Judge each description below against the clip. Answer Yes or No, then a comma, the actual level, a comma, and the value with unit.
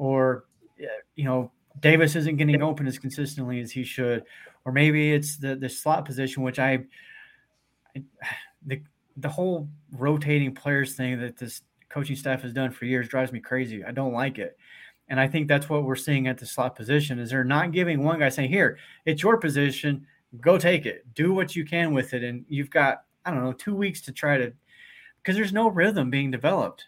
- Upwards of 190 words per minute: Yes, fast, 205 wpm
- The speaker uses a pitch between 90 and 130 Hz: No, medium, 140 Hz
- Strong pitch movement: No, average, 3.0 semitones